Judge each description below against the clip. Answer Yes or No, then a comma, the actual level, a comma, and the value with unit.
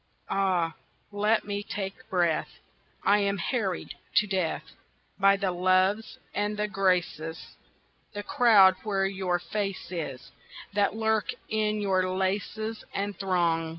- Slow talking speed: Yes, slow, 125 wpm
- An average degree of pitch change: No, narrow, 2.2 semitones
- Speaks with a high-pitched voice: Yes, high, 195 Hz